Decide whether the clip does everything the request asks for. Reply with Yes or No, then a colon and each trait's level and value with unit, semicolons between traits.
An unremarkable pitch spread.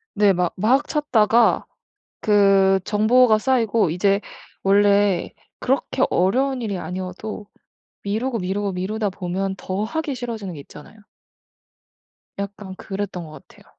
Yes: average, 3.0 semitones